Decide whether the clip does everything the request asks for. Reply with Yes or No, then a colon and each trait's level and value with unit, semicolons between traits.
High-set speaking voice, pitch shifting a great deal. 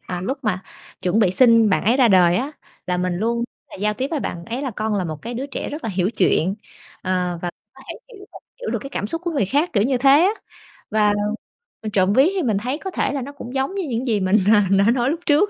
Yes: high, 230 Hz; wide, 6.2 semitones